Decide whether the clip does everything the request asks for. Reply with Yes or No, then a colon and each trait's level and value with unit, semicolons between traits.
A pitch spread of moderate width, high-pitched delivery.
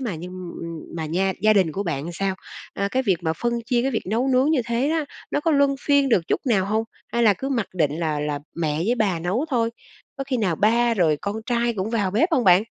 No: wide, 6.0 semitones; high, 215 Hz